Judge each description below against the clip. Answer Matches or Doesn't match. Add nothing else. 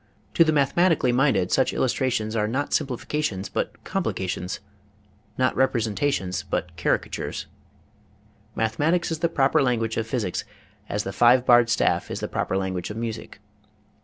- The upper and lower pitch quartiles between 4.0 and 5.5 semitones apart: Matches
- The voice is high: Doesn't match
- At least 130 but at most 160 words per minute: Matches